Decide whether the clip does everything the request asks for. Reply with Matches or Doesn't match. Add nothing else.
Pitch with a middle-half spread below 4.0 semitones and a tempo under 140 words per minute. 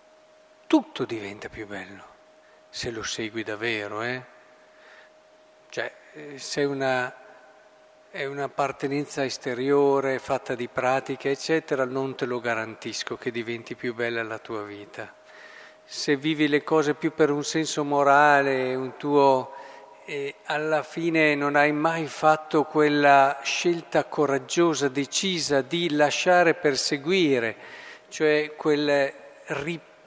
Matches